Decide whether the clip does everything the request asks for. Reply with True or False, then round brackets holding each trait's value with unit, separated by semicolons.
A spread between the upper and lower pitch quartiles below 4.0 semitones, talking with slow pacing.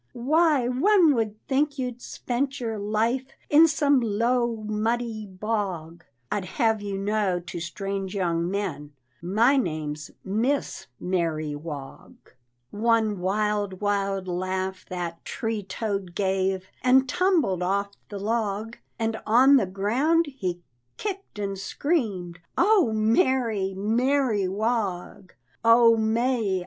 False (4.4 semitones; 120 wpm)